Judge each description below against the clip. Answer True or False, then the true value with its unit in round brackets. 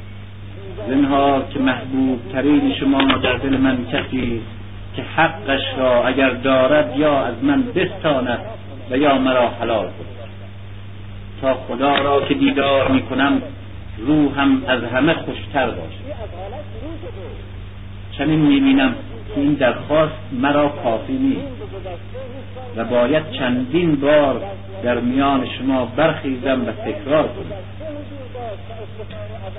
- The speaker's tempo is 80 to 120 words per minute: True (110 wpm)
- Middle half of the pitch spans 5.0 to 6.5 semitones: True (5.5 semitones)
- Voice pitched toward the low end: True (125 Hz)